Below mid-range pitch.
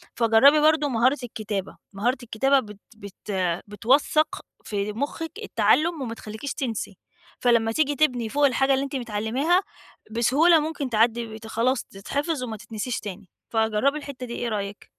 No: high, 240 Hz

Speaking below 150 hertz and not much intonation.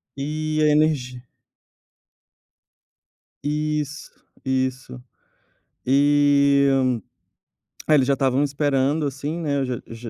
Yes: medium, 140 Hz; narrow, 2.2 semitones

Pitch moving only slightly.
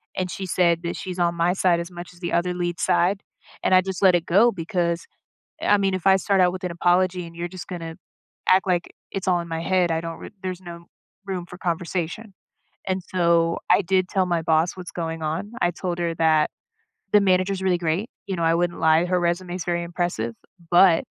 Yes: narrow, 1.6 semitones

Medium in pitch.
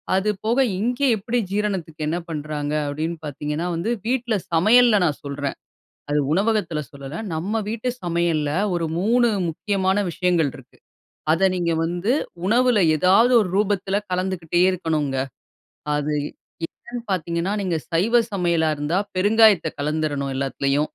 Yes: medium, 175 Hz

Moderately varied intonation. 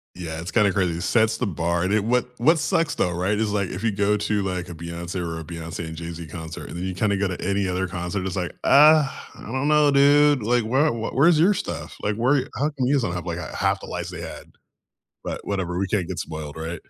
No: wide, 6.0 semitones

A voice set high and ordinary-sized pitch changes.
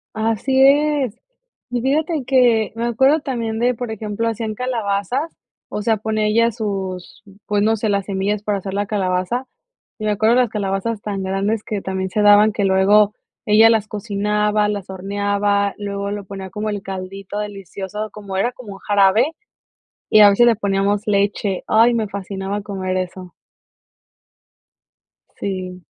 No: high, 210 Hz; narrow, 2.2 semitones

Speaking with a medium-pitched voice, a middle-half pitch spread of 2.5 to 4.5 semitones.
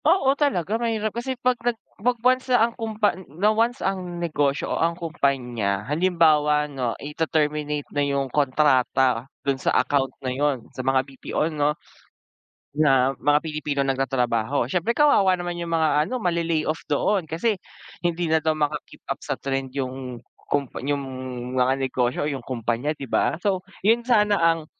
No: medium, 150 Hz; wide, 5.6 semitones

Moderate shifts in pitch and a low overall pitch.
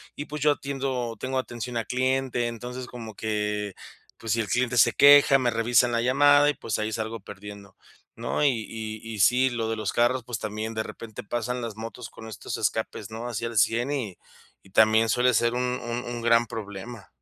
No: narrow, 2.3 semitones; low, 115 Hz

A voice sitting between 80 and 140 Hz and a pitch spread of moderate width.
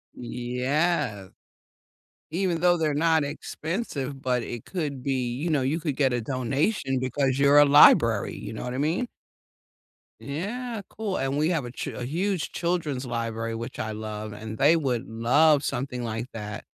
Yes: low, 135 Hz; average, 4.8 semitones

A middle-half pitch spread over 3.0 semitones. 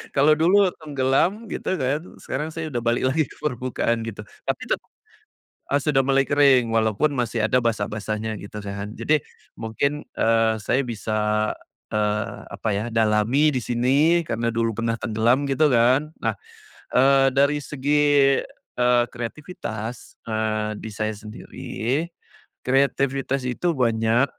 Yes: average, 4.1 semitones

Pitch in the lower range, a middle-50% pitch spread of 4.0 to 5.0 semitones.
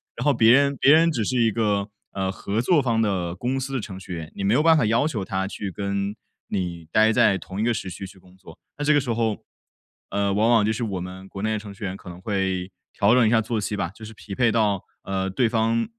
No: low, 105 Hz; average, 3.4 semitones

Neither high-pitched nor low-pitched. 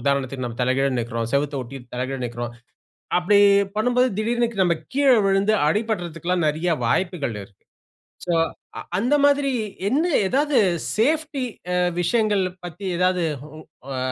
Yes: medium, 180 Hz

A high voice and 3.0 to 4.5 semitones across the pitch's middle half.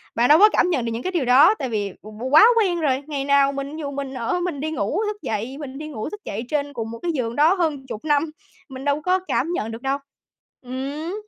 Yes: very high, 280 Hz; average, 4.0 semitones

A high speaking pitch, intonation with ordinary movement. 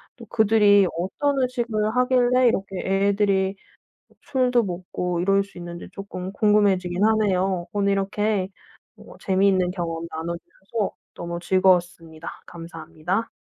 Yes: high, 195 Hz; average, 3.2 semitones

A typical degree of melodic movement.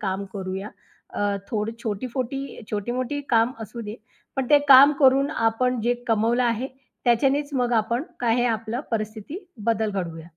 Yes: average, 3.0 semitones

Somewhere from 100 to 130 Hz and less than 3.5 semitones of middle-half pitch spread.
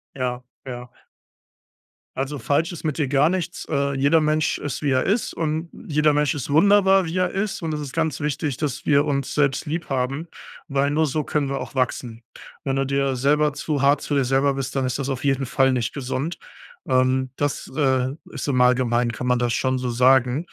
No: medium, 140 Hz; average, 2.7 semitones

